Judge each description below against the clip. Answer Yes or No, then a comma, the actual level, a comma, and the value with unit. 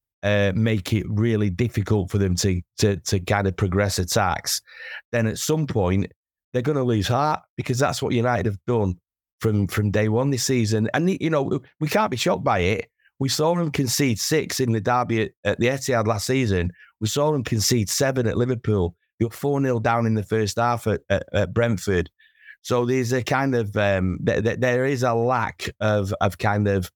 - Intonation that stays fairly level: No, average, 3.9 semitones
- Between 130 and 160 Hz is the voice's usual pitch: No, low, 115 Hz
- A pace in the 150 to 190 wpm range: No, fast, 205 wpm